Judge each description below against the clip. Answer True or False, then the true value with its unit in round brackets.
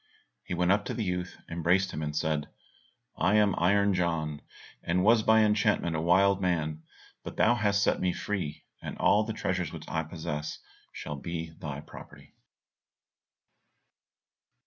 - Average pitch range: True (4.0 semitones)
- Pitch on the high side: False (90 Hz)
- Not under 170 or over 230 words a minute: False (150 wpm)